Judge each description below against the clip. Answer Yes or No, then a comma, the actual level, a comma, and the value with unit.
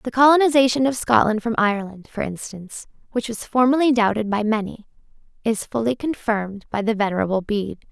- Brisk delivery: No, average, 160 wpm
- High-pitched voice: Yes, high, 225 Hz